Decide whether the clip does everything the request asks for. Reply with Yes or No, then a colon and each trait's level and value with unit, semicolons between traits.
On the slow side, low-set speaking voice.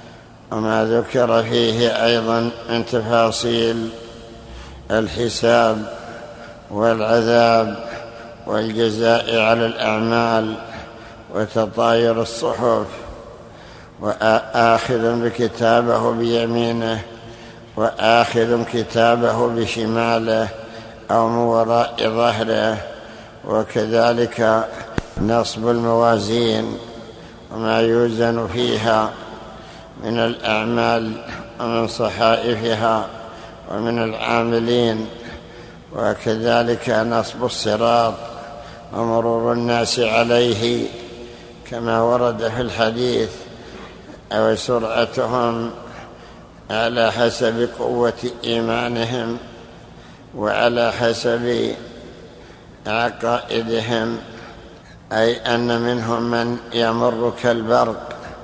Yes: slow, 60 wpm; low, 115 Hz